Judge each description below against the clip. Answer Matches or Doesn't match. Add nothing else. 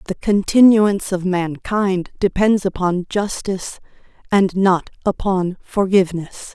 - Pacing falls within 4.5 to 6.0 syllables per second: Doesn't match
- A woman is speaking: Matches